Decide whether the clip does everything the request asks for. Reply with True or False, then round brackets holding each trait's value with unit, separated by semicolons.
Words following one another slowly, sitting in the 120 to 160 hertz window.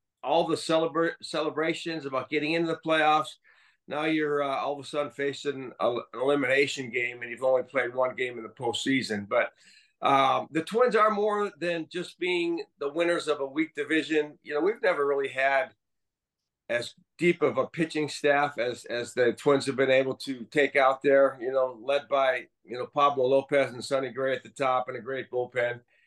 False (200 wpm; 140 Hz)